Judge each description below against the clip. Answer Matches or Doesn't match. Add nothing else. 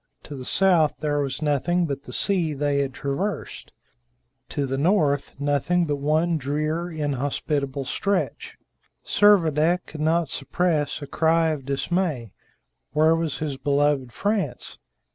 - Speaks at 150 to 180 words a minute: Doesn't match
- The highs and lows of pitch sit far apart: Doesn't match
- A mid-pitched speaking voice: Matches